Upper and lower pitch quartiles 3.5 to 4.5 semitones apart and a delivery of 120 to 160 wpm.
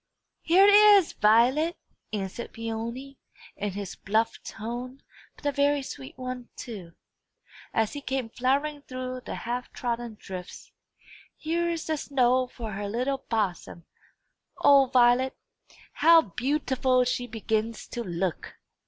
Yes: average, 3.9 semitones; slow, 135 wpm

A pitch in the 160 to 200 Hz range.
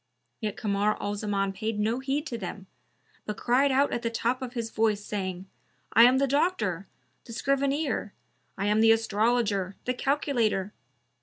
No: high, 225 Hz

